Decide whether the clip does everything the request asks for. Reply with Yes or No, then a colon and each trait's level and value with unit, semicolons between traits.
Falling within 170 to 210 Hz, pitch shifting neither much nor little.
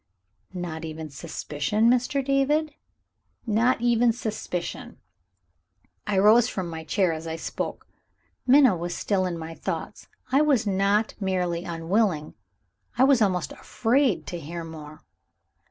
No: high, 190 Hz; wide, 6.4 semitones